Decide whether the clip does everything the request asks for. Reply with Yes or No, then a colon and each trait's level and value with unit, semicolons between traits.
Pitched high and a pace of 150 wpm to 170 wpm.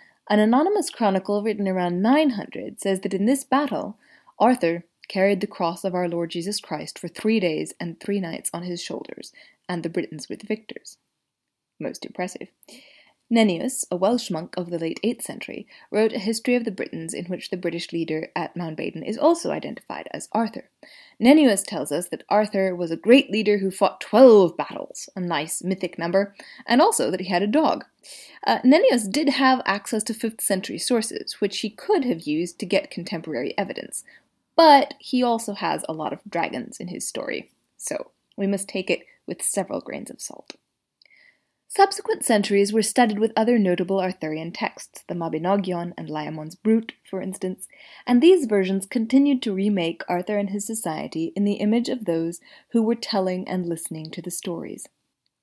No: high, 200 Hz; average, 180 wpm